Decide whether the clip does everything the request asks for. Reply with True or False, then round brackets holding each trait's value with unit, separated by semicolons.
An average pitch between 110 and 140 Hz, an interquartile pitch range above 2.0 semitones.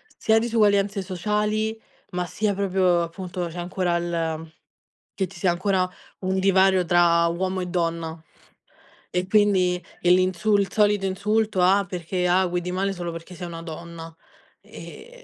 False (185 Hz; 2.4 semitones)